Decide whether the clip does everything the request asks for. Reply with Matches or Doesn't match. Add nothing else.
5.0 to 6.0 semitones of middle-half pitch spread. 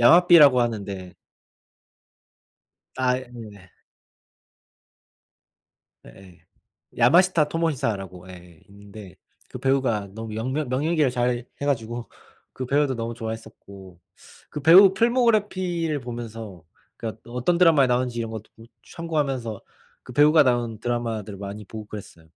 Matches